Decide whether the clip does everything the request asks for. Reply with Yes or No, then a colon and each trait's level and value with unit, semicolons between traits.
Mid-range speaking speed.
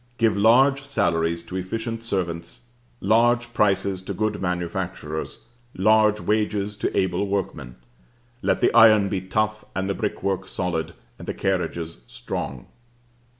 No: slow, 130 wpm